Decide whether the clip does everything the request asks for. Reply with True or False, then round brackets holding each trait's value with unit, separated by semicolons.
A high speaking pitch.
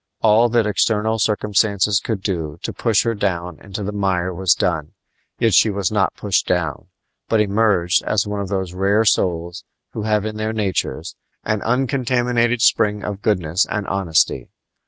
False (105 Hz)